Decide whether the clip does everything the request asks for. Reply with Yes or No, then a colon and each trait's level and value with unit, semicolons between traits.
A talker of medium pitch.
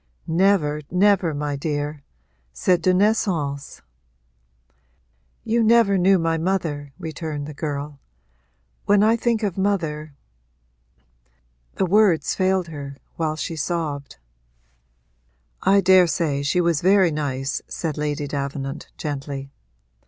Yes: medium, 155 Hz